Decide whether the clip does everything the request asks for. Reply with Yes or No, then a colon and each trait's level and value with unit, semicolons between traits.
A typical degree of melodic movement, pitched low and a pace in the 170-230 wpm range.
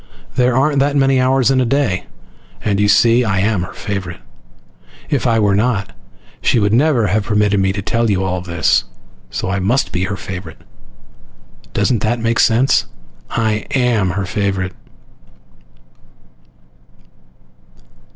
No: average, 4.2 semitones; low, 105 Hz; average, 145 wpm